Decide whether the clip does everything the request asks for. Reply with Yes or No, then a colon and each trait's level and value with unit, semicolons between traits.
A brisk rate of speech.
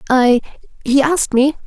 No: slow, 110 wpm